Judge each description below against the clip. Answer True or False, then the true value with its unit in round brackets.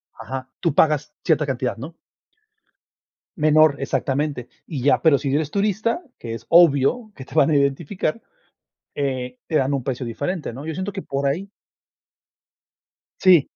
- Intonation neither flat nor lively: True (3.5 semitones)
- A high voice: False (145 Hz)